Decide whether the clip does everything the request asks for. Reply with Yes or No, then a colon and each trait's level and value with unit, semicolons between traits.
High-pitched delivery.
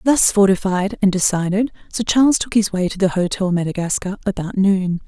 Yes: high, 195 Hz